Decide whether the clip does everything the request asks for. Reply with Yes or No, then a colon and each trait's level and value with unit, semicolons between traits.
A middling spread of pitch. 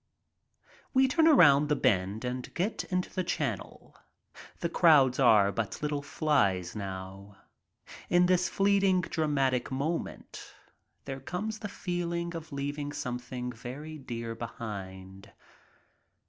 No: wide, 6.9 semitones